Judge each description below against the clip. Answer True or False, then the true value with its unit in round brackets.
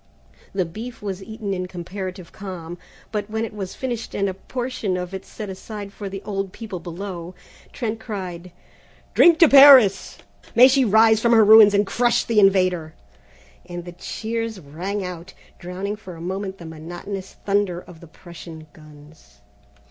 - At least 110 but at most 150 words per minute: False (165 wpm)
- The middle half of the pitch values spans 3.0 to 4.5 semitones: True (3.6 semitones)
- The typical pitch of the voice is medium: False (195 Hz)